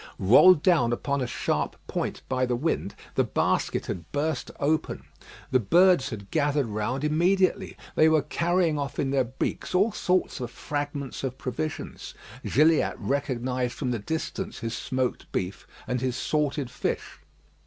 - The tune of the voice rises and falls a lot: No, average, 4.2 semitones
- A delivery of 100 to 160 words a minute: Yes, average, 155 wpm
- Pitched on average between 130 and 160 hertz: Yes, medium, 140 Hz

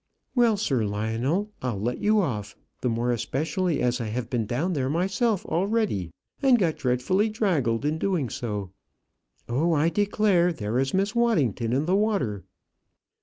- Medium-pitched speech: Yes, medium, 150 Hz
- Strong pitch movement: Yes, wide, 8.7 semitones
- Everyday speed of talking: Yes, average, 160 wpm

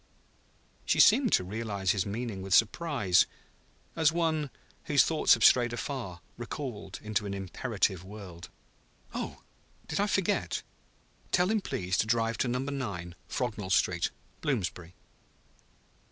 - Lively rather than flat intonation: Yes, wide, 6.7 semitones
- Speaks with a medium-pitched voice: No, low, 110 Hz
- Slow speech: Yes, slow, 130 wpm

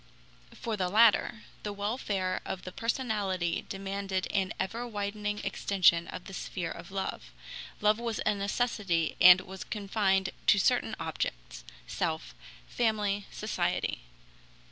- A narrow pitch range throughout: Yes, narrow, 2.3 semitones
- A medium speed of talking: No, slow, 125 wpm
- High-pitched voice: Yes, high, 200 Hz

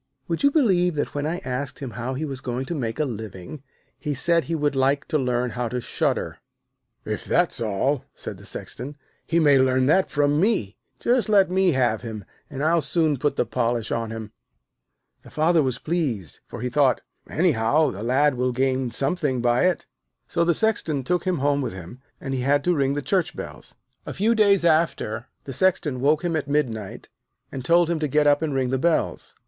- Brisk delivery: Yes, fast, 210 wpm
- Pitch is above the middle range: No, medium, 140 Hz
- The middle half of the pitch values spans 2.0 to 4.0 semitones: No, average, 4.7 semitones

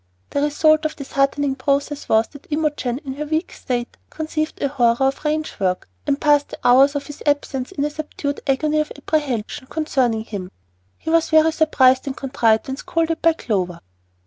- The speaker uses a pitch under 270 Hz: No, very high, 285 Hz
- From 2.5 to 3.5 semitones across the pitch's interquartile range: Yes, average, 3.0 semitones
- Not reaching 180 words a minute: No, average, 185 wpm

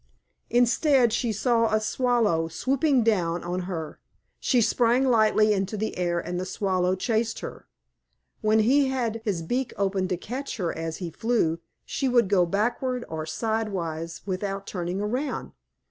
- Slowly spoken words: No, average, 155 wpm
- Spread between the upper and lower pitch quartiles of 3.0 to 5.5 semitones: Yes, average, 5.0 semitones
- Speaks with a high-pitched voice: Yes, high, 215 Hz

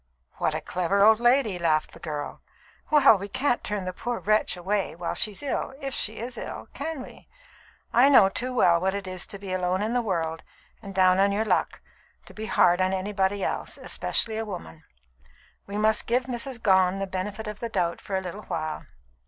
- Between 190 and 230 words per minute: Yes, fast, 205 wpm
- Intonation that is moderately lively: Yes, average, 3.5 semitones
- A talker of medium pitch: No, high, 200 Hz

